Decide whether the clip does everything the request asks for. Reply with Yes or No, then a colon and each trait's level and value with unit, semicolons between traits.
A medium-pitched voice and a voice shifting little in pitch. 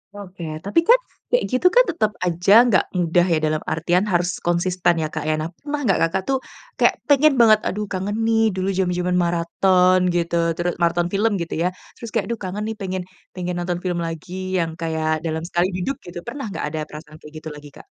No: medium, 180 Hz; average, 3.1 semitones